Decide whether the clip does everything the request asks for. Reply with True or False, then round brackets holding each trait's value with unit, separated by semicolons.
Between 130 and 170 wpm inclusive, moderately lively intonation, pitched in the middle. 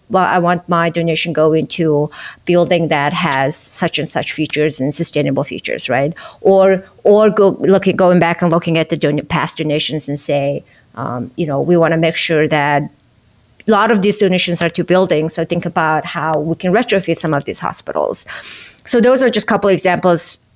False (200 wpm; 3.3 semitones; 165 Hz)